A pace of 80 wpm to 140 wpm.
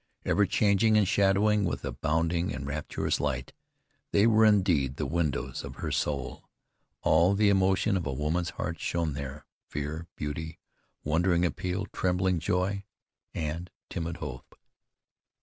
Yes: slow, 135 wpm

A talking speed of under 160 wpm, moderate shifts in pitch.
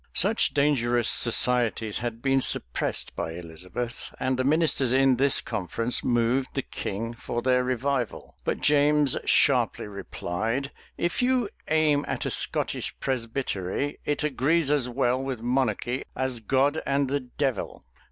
Yes: average, 140 wpm; average, 3.1 semitones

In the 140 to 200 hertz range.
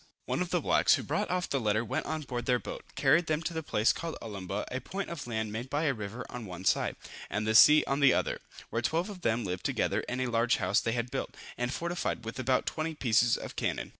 No: low, 125 Hz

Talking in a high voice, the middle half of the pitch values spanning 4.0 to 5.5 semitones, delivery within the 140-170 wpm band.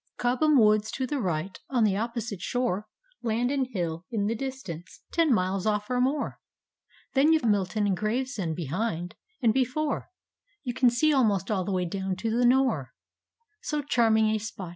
No: high, 225 Hz; average, 5.1 semitones; average, 185 wpm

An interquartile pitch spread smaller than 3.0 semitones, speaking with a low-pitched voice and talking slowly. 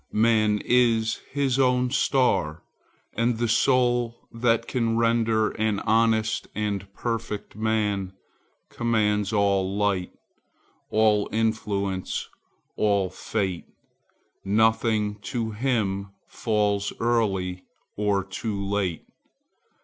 Yes: narrow, 2.4 semitones; low, 110 Hz; slow, 95 wpm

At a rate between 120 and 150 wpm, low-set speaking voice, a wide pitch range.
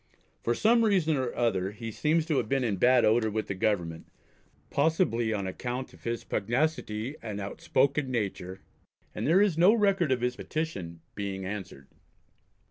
No: average, 165 wpm; low, 120 Hz; wide, 7.2 semitones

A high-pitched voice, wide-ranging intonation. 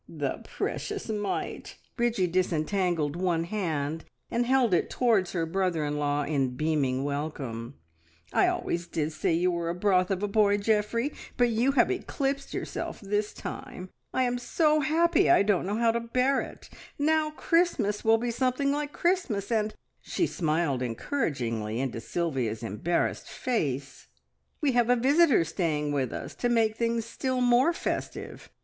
Yes: high, 200 Hz; wide, 7.8 semitones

